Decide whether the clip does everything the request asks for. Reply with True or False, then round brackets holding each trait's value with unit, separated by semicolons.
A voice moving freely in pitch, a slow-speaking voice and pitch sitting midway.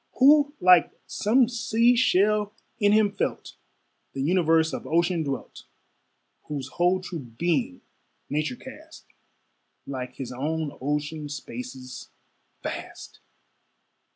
True (7.1 semitones; 105 wpm; 175 Hz)